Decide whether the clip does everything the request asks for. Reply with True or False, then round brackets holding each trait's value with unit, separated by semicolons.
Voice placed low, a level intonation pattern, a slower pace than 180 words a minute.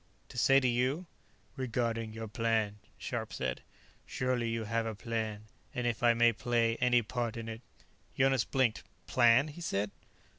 True (115 Hz; 1.9 semitones; 170 wpm)